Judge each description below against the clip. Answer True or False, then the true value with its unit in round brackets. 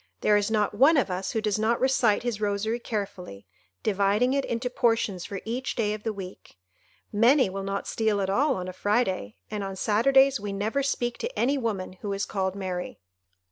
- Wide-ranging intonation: False (3.5 semitones)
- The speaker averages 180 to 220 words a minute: True (200 wpm)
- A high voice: True (210 Hz)